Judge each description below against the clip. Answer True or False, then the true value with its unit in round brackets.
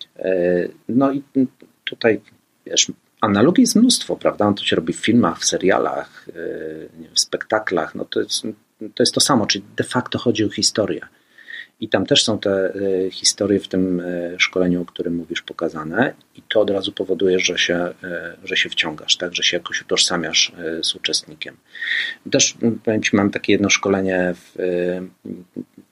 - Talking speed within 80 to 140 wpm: False (155 wpm)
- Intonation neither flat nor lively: False (6.6 semitones)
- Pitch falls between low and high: False (95 Hz)